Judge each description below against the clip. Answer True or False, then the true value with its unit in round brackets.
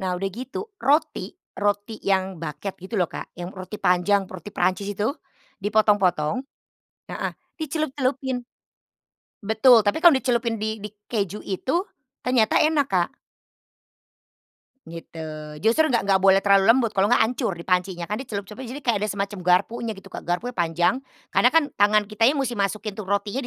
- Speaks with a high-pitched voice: True (205 Hz)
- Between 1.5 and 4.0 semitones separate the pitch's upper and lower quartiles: False (4.5 semitones)